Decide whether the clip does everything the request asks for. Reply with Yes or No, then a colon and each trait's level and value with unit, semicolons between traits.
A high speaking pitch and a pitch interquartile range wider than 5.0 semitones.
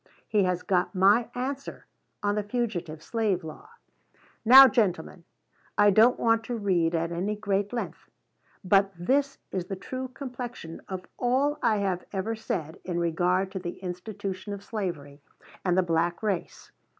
No: high, 195 Hz; average, 4.3 semitones